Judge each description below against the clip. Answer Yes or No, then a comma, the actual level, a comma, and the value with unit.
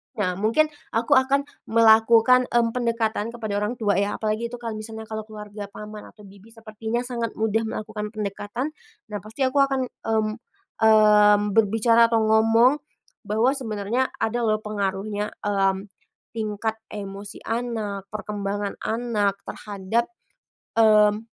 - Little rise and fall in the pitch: Yes, narrow, 1.9 semitones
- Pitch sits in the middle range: No, high, 220 Hz